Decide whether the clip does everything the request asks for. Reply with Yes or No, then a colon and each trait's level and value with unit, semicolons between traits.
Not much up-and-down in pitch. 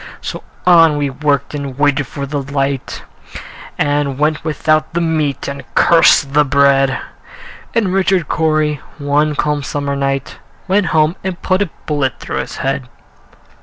Yes: narrow, 2.2 semitones